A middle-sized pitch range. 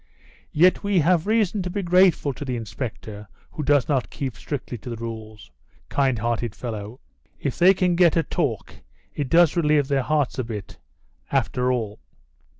No: wide, 6.6 semitones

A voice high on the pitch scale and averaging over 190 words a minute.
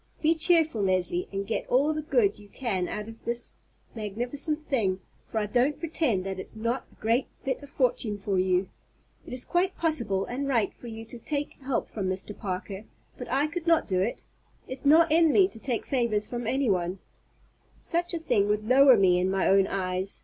Yes: high, 235 Hz; average, 200 wpm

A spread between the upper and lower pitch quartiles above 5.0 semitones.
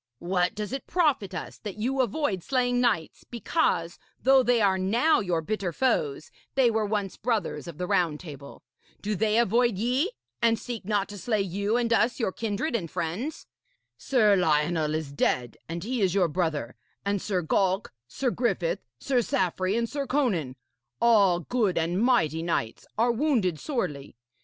Yes: wide, 5.6 semitones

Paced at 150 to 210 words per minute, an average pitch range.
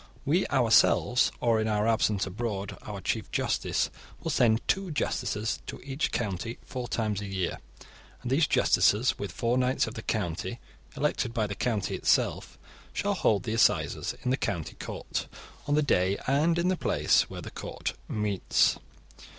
Yes: average, 165 wpm; average, 4.1 semitones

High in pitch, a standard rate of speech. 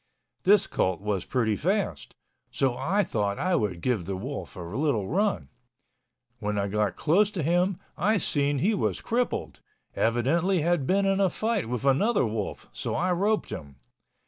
No: medium, 140 Hz; average, 170 wpm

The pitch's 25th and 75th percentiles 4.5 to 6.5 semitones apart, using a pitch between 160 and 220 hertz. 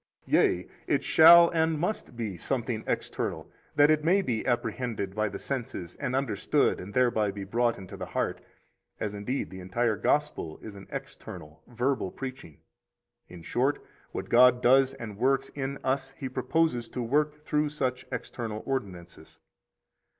No: average, 4.9 semitones; low, 125 Hz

